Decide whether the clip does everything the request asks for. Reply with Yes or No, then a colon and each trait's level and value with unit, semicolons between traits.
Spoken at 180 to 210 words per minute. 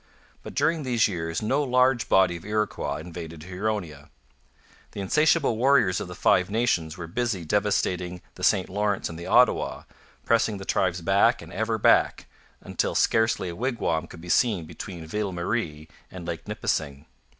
No: average, 160 wpm